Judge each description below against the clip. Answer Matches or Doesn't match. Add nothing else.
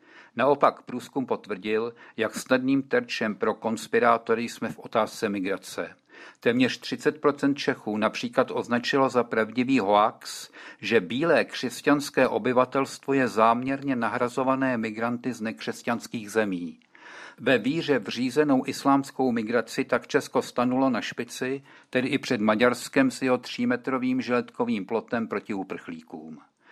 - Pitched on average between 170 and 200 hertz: Doesn't match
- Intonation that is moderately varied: Doesn't match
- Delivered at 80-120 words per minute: Matches